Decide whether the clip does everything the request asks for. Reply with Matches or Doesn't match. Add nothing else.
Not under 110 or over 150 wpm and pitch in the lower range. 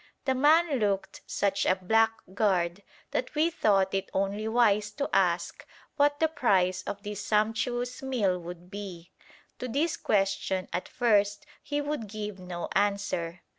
Doesn't match